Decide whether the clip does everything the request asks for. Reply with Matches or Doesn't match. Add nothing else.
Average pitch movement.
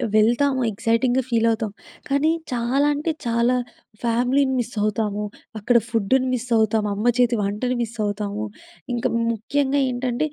Matches